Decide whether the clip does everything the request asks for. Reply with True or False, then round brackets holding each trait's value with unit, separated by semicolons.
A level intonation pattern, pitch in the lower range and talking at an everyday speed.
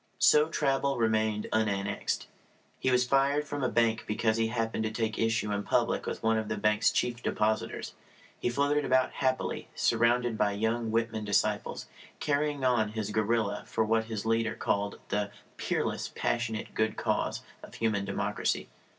True (2.3 semitones; 115 Hz; 160 wpm)